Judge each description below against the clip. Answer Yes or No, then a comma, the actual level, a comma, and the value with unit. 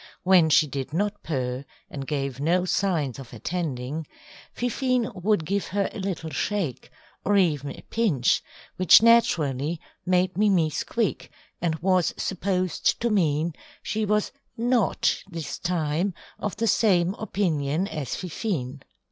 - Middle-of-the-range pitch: Yes, medium, 175 Hz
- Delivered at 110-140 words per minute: Yes, slow, 135 wpm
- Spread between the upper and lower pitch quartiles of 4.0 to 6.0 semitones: Yes, average, 5.1 semitones